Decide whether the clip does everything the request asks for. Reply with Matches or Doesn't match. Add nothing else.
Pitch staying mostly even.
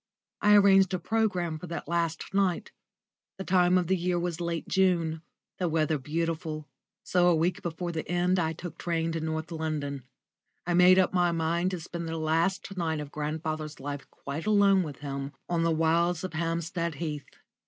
Matches